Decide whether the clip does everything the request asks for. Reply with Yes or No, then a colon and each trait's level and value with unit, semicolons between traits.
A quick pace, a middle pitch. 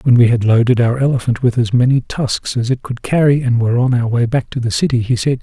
No: fast, 275 wpm; low, 125 Hz